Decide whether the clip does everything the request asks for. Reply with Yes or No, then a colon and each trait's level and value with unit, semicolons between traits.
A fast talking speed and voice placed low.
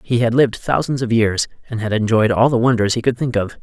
Yes: fast, 265 wpm; low, 115 Hz